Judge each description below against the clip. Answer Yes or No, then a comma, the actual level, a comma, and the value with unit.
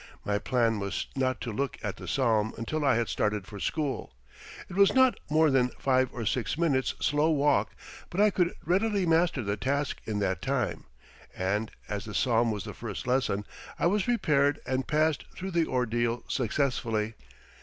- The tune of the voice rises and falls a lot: Yes, wide, 6.0 semitones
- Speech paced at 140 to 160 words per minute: No, average, 180 wpm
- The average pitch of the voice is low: Yes, low, 130 Hz